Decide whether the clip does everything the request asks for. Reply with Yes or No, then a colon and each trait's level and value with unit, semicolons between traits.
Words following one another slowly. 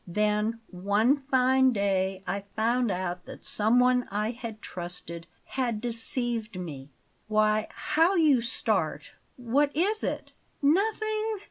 Yes: slow, 120 wpm